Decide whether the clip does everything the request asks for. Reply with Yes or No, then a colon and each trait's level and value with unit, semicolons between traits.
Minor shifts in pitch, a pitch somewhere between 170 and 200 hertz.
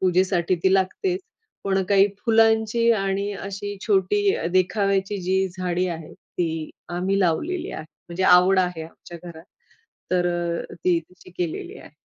Yes: narrow, 2.3 semitones; medium, 185 Hz